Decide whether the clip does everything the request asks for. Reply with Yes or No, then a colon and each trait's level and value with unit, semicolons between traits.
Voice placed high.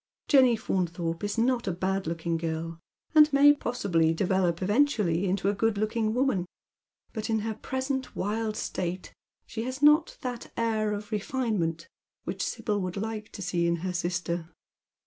Yes: high, 205 Hz